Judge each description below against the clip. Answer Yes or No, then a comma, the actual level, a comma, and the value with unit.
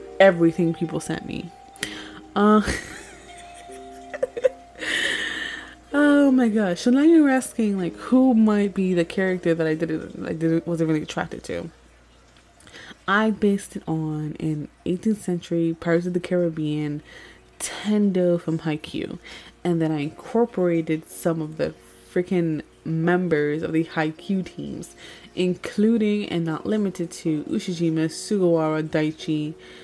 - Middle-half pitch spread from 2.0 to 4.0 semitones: No, average, 5.1 semitones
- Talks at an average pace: No, slow, 125 wpm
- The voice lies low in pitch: No, medium, 175 Hz